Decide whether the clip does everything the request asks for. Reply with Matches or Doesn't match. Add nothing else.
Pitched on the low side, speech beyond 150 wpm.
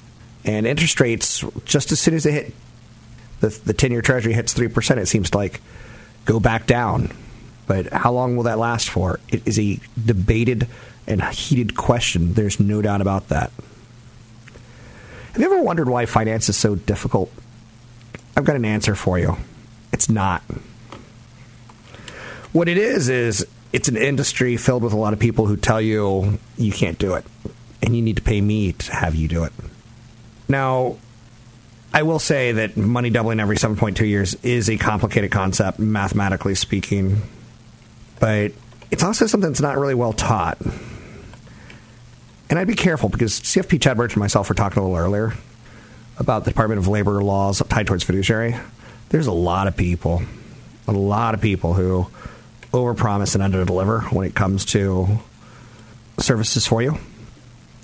Matches